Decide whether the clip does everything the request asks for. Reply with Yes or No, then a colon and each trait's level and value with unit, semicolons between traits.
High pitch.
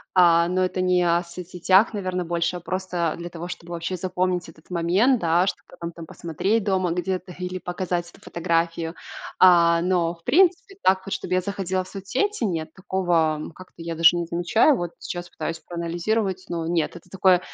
No: medium, 175 Hz